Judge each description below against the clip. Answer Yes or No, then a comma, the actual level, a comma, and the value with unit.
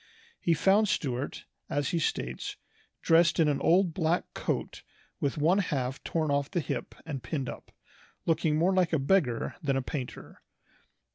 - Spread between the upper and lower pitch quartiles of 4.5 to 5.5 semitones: No, average, 3.7 semitones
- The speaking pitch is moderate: Yes, medium, 155 Hz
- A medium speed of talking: Yes, average, 160 wpm